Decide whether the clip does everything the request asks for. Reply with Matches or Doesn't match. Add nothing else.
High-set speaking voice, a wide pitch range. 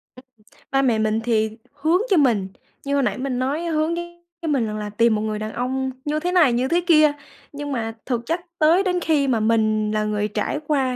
Matches